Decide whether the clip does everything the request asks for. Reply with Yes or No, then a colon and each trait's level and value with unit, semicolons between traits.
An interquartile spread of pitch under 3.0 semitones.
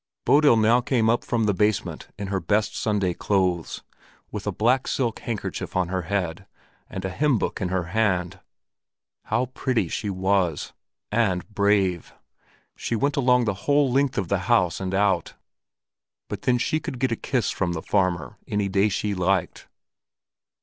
No: average, 4.1 semitones